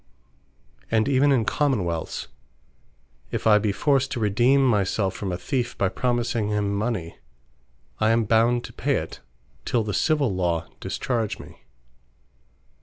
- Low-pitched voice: Yes, low, 110 Hz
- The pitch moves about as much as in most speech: Yes, average, 3.8 semitones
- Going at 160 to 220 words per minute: No, average, 150 wpm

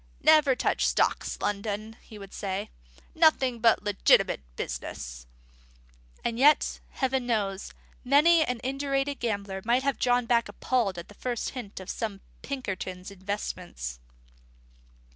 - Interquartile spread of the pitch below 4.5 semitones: No, average, 5.2 semitones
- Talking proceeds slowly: Yes, slow, 130 wpm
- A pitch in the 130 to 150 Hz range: No, high, 225 Hz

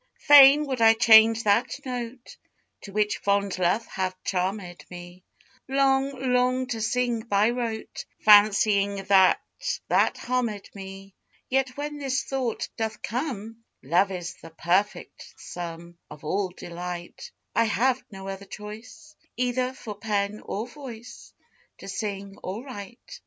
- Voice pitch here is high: Yes, high, 215 Hz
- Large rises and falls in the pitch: No, average, 4.3 semitones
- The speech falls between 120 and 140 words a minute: Yes, slow, 135 wpm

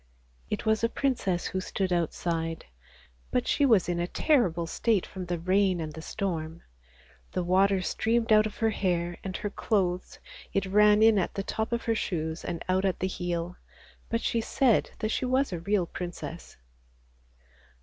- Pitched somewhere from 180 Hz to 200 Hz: Yes, high, 190 Hz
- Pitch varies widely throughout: No, average, 3.9 semitones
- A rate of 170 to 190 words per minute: Yes, average, 180 wpm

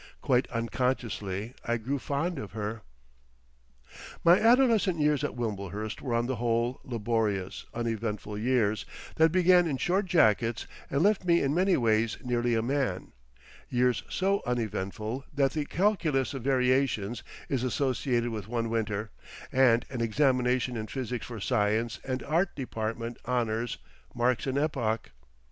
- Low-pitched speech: Yes, low, 120 Hz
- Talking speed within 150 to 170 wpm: No, average, 140 wpm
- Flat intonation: No, average, 3.8 semitones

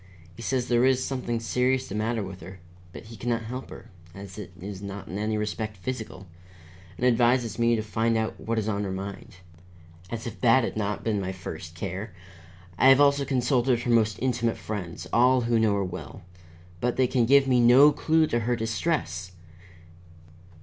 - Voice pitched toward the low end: Yes, low, 115 Hz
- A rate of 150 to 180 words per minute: No, average, 195 wpm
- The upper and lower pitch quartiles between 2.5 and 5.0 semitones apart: Yes, average, 3.6 semitones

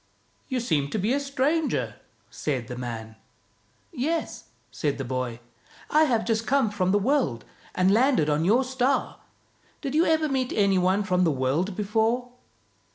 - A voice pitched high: Yes, high, 210 Hz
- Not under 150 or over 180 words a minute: Yes, average, 170 wpm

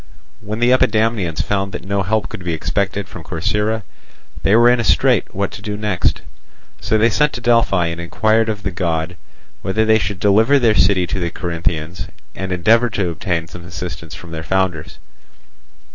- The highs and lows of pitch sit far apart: No, average, 4.2 semitones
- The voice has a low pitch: Yes, very low, 95 Hz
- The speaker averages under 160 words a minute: No, average, 185 wpm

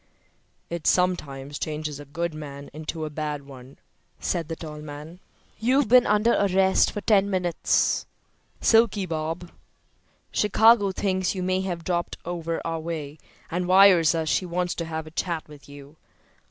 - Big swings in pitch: No, average, 3.6 semitones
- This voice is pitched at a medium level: Yes, medium, 170 Hz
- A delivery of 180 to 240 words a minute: No, average, 155 wpm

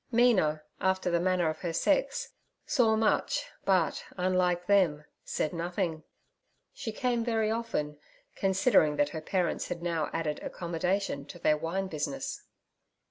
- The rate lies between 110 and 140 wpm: Yes, slow, 135 wpm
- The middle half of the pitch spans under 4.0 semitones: No, average, 4.7 semitones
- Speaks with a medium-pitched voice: Yes, medium, 180 Hz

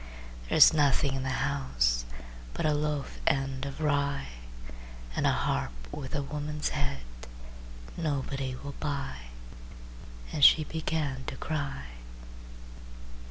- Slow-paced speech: Yes, slow, 115 wpm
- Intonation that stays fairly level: Yes, narrow, 1.9 semitones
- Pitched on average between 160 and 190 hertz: No, medium, 140 Hz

